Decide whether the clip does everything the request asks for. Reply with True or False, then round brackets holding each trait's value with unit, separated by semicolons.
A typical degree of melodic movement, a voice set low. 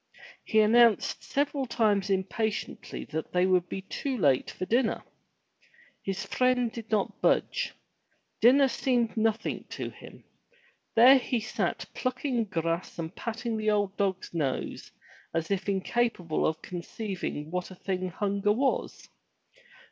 False (4.4 semitones; 210 Hz)